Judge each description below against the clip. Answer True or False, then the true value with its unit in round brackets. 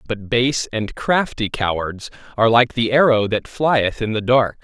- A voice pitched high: False (115 Hz)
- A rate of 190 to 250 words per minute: False (180 wpm)